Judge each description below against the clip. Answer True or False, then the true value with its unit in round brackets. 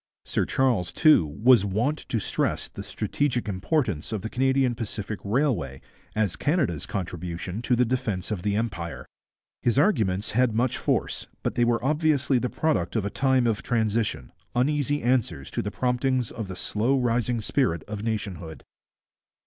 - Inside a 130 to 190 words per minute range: True (160 wpm)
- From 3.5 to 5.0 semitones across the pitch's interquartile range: True (4.7 semitones)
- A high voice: False (115 Hz)